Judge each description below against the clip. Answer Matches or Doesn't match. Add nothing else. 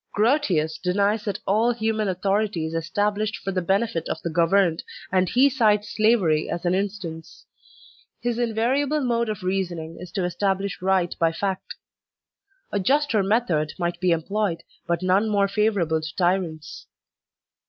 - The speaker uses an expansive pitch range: Doesn't match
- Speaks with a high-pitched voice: Matches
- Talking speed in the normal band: Matches